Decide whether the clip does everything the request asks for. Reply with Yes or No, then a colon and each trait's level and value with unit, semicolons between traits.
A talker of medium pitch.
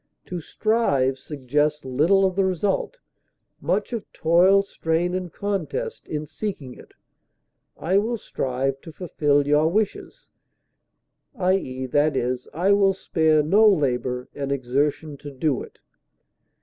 Yes: medium, 160 Hz